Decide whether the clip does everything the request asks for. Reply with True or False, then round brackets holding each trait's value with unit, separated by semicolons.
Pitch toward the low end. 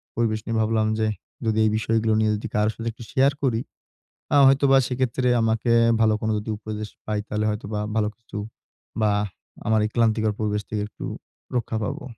True (110 Hz)